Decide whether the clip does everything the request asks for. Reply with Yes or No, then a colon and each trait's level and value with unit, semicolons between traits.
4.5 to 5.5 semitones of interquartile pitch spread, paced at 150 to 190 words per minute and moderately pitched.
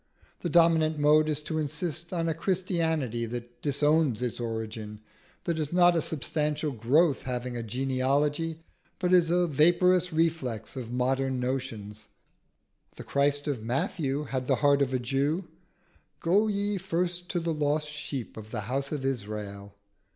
Yes: average, 4.8 semitones; average, 155 wpm; medium, 145 Hz